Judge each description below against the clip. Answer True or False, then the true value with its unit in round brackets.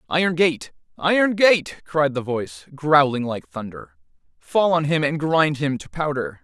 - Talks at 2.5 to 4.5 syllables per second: True (4.4 syllables/s)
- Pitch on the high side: False (155 Hz)